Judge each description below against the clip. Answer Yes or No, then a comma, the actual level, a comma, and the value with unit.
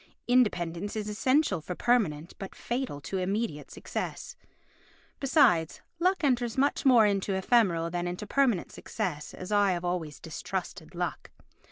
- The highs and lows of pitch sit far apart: Yes, wide, 5.8 semitones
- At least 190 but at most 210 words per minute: No, average, 140 wpm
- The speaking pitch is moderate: No, high, 205 Hz